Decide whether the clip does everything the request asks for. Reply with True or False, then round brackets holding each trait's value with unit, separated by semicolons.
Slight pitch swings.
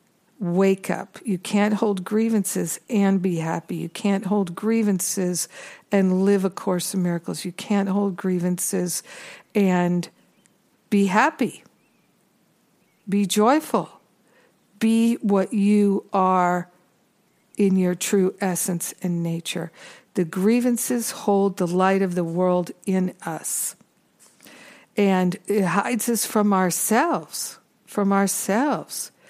True (2.3 semitones)